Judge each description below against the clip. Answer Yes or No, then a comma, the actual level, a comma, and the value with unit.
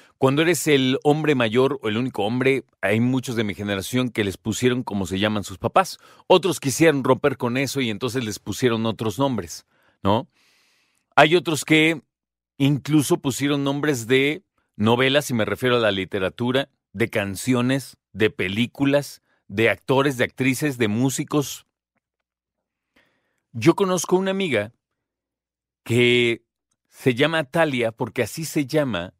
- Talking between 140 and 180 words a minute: Yes, average, 145 wpm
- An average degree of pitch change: Yes, average, 4.1 semitones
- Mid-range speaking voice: No, low, 130 Hz